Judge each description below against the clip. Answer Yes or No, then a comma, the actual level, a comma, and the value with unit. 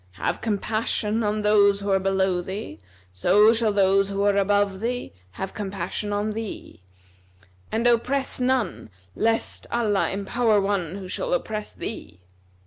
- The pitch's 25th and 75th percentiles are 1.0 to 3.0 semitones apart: Yes, narrow, 2.4 semitones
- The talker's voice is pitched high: Yes, high, 205 Hz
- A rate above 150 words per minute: No, average, 140 wpm